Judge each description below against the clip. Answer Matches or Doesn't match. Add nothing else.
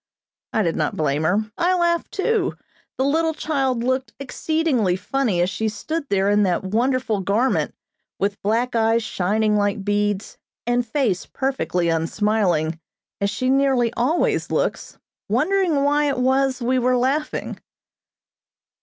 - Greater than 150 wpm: Doesn't match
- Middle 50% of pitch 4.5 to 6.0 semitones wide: Matches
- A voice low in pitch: Doesn't match